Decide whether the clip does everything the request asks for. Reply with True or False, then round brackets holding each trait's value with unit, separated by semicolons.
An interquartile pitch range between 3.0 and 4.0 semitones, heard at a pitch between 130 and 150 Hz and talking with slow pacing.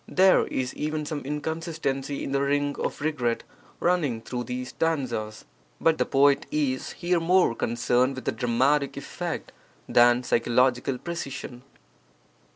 True (3.7 semitones; 135 Hz; 130 wpm)